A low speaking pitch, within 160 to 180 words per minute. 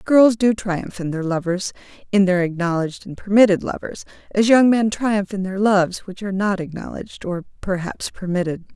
No: high, 195 Hz; average, 170 wpm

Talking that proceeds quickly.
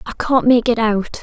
Yes: fast, 245 wpm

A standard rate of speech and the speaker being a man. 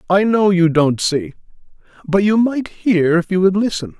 Yes: average, 195 wpm; male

